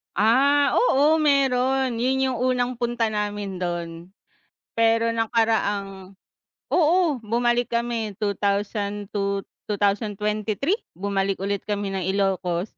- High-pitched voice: Yes, high, 215 Hz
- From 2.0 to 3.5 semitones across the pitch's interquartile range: No, average, 3.9 semitones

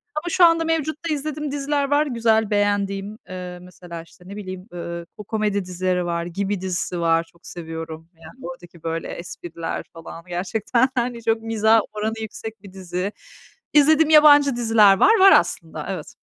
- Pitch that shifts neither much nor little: No, wide, 6.8 semitones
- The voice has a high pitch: Yes, high, 205 Hz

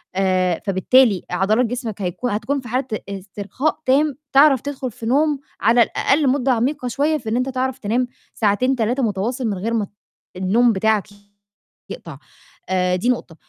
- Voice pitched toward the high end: Yes, high, 235 Hz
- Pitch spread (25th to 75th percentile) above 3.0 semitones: Yes, average, 4.5 semitones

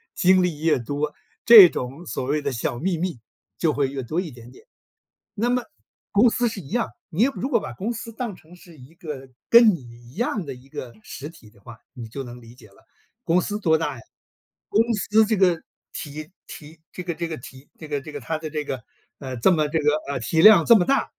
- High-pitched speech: No, medium, 155 Hz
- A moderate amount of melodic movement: No, wide, 6.1 semitones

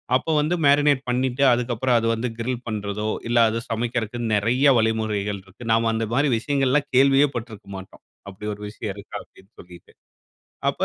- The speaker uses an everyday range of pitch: Yes, average, 3.5 semitones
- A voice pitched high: No, low, 115 Hz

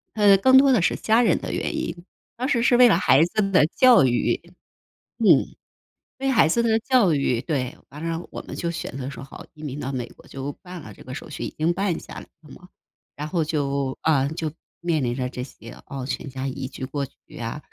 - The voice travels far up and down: Yes, wide, 6.5 semitones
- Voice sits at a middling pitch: Yes, medium, 155 Hz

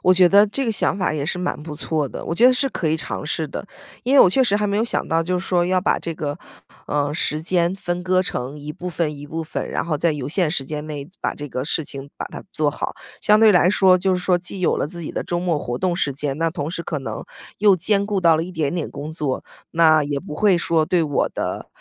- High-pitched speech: No, medium, 170 Hz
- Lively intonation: No, average, 3.5 semitones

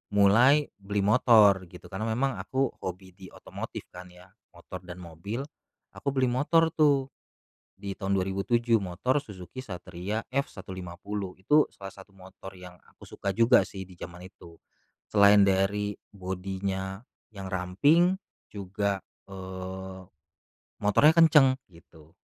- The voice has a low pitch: Yes, low, 100 Hz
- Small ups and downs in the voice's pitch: No, average, 3.8 semitones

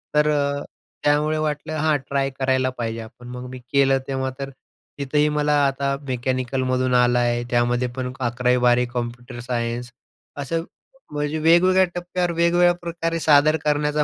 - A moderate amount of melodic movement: Yes, average, 3.4 semitones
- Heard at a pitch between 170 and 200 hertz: No, low, 135 Hz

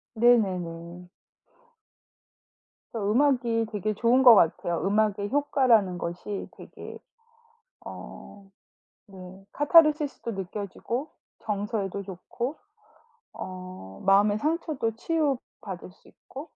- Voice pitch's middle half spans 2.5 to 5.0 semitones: No, wide, 5.5 semitones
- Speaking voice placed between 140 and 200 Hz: No, high, 210 Hz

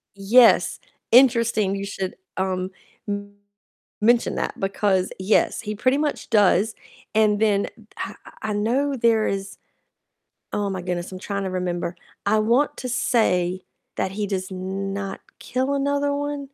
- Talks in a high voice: Yes, high, 205 Hz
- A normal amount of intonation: Yes, average, 3.8 semitones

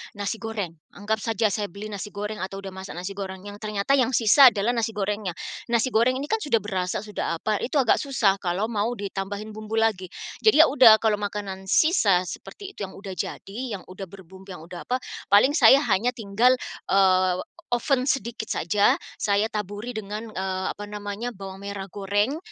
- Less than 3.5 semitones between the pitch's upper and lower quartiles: Yes, average, 2.9 semitones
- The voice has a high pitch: Yes, high, 205 Hz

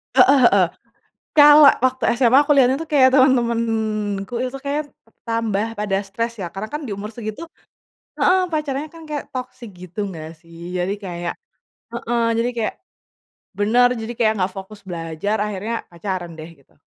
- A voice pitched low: No, high, 220 Hz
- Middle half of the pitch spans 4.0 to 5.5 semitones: Yes, average, 5.0 semitones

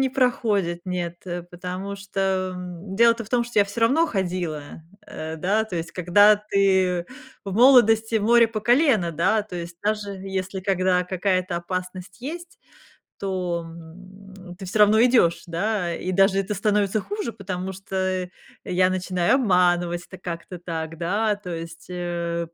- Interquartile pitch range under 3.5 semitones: Yes, average, 2.9 semitones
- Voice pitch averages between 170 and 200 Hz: Yes, high, 190 Hz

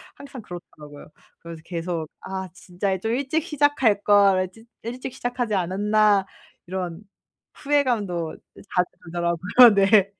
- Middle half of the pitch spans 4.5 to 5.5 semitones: Yes, average, 5.1 semitones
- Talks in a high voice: Yes, high, 200 Hz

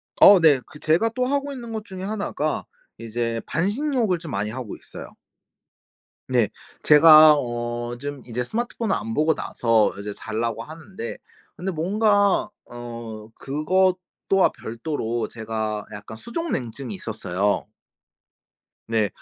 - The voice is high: No, medium, 145 Hz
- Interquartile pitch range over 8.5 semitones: Yes, wide, 9.0 semitones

